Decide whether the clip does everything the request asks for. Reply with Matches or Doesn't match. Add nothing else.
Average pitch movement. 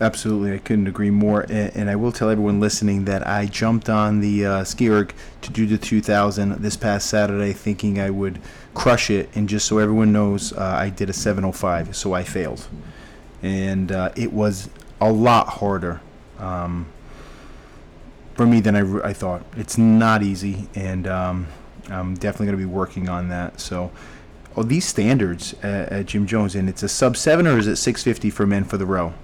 Doesn't match